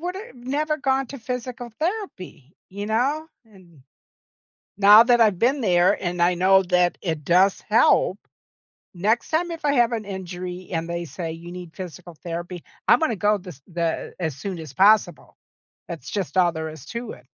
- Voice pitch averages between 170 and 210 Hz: Yes, high, 190 Hz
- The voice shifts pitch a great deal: Yes, wide, 5.7 semitones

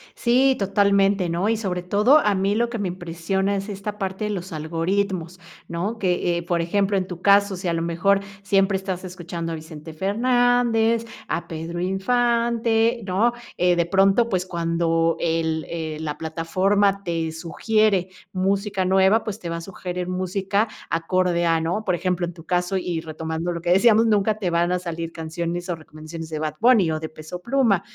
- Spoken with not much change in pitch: No, average, 3.3 semitones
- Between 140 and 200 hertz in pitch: Yes, medium, 185 Hz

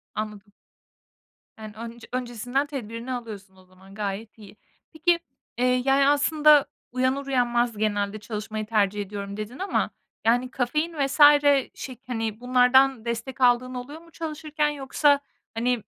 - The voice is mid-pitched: No, high, 245 Hz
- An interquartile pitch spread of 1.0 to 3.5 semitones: No, average, 4.0 semitones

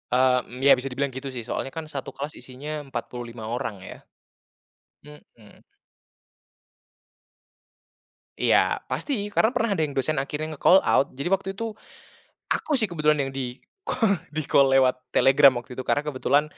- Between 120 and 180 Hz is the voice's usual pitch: Yes, medium, 140 Hz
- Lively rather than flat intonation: No, average, 3.4 semitones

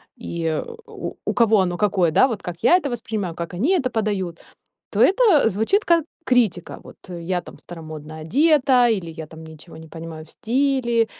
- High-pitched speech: Yes, high, 200 Hz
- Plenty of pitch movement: Yes, wide, 7.1 semitones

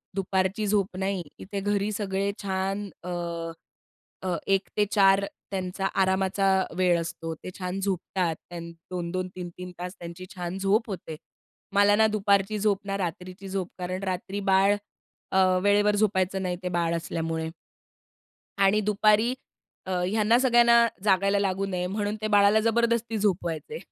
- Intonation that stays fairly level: Yes, narrow, 2.1 semitones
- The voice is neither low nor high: No, high, 195 Hz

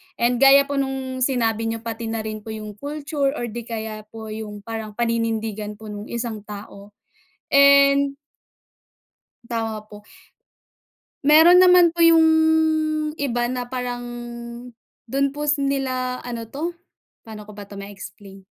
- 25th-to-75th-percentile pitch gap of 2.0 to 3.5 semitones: No, average, 4.3 semitones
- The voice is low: No, high, 235 Hz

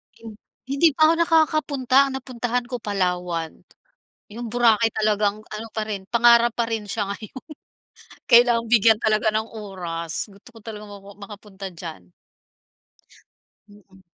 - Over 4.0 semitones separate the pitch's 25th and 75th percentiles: No, average, 3.0 semitones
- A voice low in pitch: No, high, 220 Hz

